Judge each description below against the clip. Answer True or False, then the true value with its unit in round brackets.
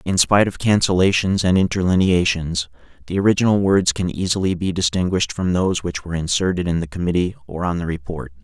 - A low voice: True (90 Hz)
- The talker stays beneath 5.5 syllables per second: False (6.2 syllables/s)